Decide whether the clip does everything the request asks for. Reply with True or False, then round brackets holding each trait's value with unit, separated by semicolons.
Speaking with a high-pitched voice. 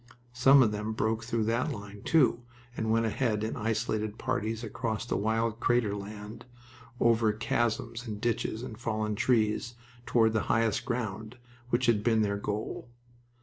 False (110 Hz)